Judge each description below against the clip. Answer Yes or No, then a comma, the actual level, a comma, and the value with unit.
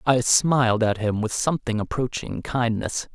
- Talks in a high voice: No, low, 120 Hz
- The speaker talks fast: No, average, 155 wpm